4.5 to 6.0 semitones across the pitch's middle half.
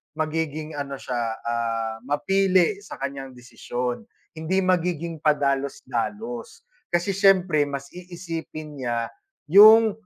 Yes: average, 5.2 semitones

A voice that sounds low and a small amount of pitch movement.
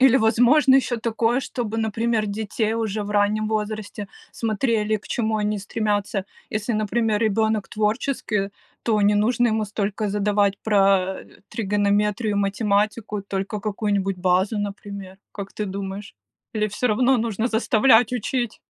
No: high, 210 Hz; narrow, 1.8 semitones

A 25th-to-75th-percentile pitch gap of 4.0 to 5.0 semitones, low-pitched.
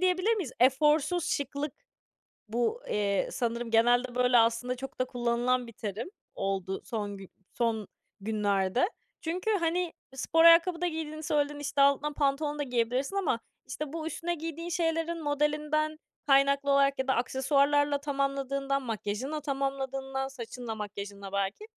No: average, 4.4 semitones; very high, 275 Hz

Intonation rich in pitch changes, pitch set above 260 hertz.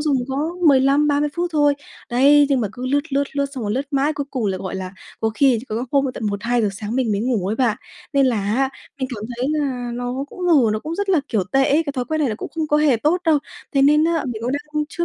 No: average, 3.7 semitones; very high, 270 Hz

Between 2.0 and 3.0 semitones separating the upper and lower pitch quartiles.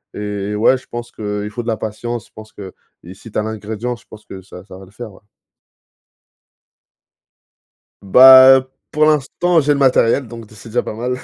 No: average, 3.4 semitones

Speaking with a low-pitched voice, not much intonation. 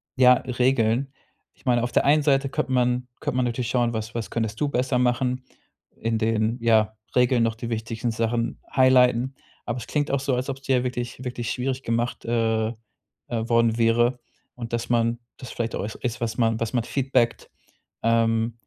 Yes: low, 120 Hz; narrow, 1.8 semitones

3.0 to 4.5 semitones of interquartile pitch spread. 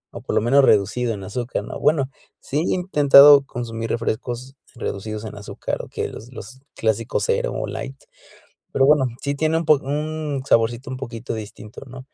Yes: average, 4.0 semitones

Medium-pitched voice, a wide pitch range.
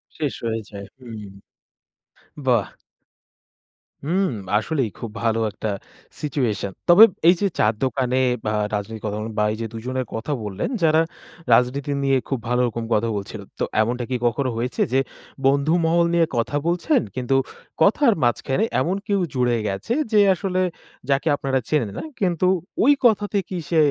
No: low, 130 Hz; wide, 6.7 semitones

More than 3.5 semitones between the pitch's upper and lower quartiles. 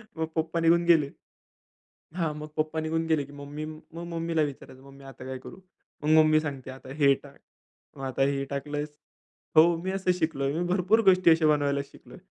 No: average, 2.9 semitones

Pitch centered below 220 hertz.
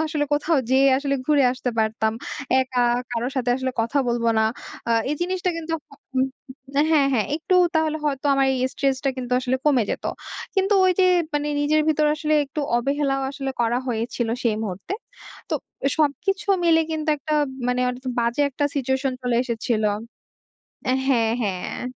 No: very high, 270 Hz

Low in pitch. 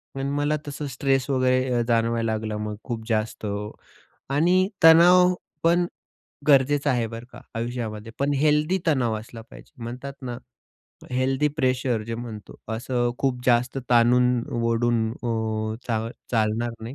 Yes: low, 125 Hz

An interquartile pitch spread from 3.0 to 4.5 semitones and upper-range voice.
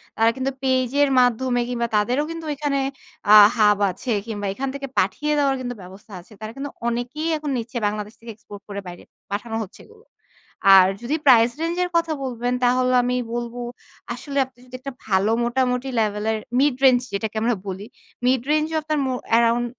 Yes: average, 3.6 semitones; high, 245 Hz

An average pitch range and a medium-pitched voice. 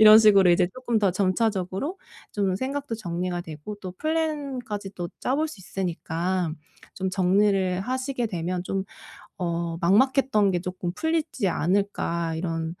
No: average, 4.4 semitones; high, 195 Hz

